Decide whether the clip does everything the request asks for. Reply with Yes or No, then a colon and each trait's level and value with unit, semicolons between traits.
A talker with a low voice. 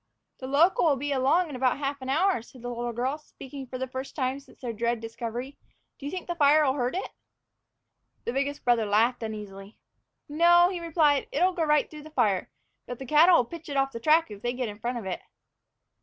No: very high, 265 Hz